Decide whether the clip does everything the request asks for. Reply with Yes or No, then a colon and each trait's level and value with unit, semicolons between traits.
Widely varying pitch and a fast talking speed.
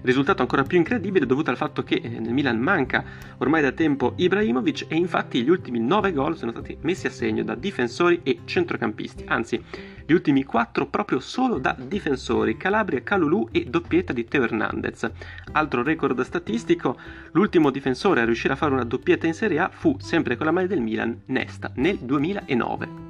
Yes: wide, 7.3 semitones; fast, 180 wpm